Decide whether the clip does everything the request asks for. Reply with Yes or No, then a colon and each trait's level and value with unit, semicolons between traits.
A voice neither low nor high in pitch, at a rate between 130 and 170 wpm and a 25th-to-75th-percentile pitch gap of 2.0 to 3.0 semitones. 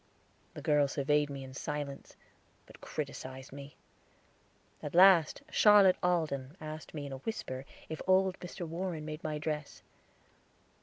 No: medium, 150 Hz; average, 140 wpm; average, 3.9 semitones